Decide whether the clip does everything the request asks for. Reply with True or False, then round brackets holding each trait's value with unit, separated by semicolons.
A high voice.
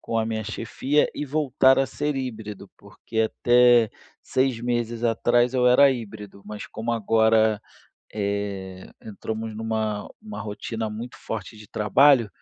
False (115 Hz)